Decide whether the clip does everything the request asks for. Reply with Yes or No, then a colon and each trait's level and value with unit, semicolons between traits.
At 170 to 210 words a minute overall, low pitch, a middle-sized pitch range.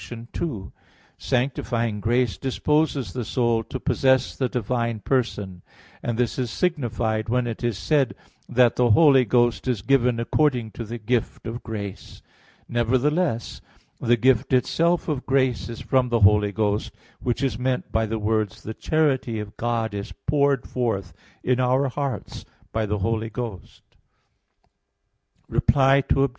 No: average, 145 wpm; low, 120 Hz; average, 3.0 semitones